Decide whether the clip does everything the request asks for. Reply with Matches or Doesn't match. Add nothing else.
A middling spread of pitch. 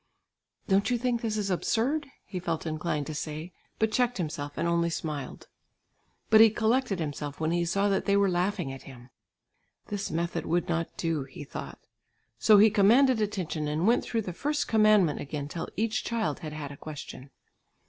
Doesn't match